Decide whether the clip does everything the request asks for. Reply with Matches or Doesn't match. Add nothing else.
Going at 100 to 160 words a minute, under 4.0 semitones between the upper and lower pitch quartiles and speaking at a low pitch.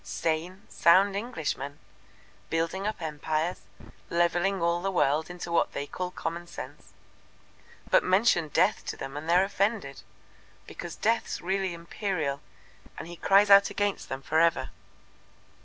Doesn't match